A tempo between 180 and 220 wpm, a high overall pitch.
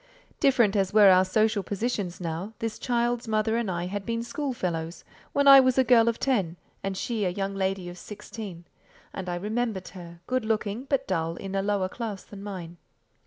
Yes: average, 195 wpm; high, 205 Hz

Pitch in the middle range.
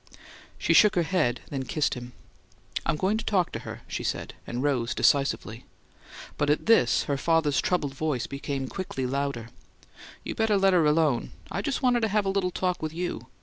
Yes: medium, 155 Hz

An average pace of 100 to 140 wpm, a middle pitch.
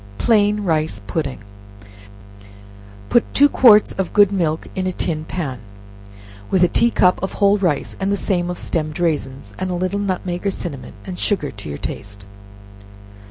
No: average, 160 wpm; medium, 180 Hz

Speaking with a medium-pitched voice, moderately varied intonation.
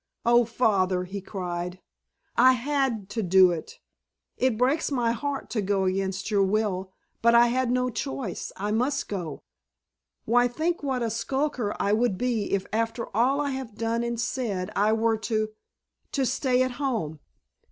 No: high, 230 Hz; average, 4.1 semitones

